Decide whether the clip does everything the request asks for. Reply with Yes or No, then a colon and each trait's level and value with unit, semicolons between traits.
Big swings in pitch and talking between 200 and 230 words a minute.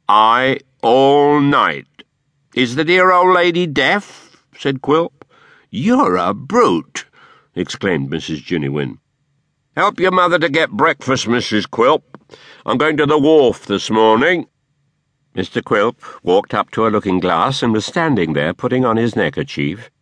No: wide, 6.1 semitones; average, 140 wpm